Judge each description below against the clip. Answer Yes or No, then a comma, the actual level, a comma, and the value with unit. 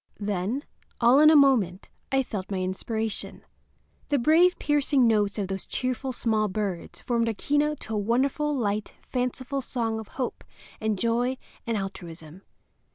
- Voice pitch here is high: Yes, high, 230 Hz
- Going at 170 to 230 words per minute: No, average, 155 wpm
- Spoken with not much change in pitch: No, average, 4.8 semitones